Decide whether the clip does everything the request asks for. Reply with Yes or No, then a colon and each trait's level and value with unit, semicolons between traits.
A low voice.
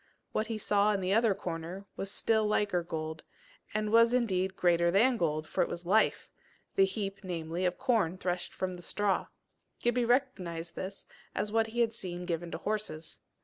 No: high, 195 Hz